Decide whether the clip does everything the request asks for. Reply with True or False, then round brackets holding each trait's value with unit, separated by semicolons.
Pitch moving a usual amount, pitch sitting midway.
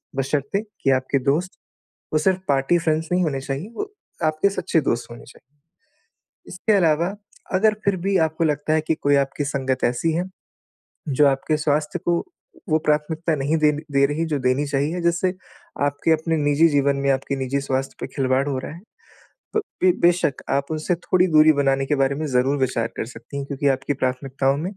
True (3.3 semitones; 145 Hz)